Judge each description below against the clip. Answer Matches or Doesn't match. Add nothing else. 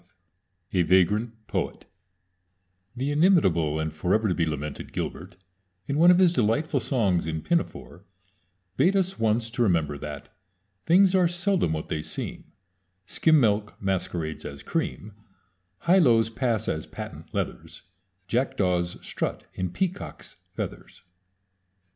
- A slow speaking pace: Matches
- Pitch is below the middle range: Matches